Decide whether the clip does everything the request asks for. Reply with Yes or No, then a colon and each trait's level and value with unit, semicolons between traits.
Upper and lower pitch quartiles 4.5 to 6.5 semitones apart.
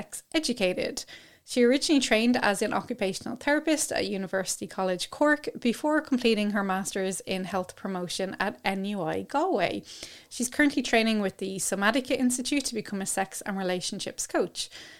Yes: average, 5.1 semitones